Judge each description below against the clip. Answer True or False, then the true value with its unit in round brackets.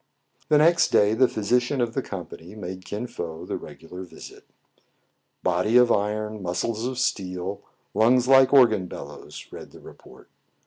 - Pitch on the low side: True (110 Hz)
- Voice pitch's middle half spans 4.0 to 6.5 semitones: True (5.1 semitones)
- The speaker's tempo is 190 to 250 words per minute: False (160 wpm)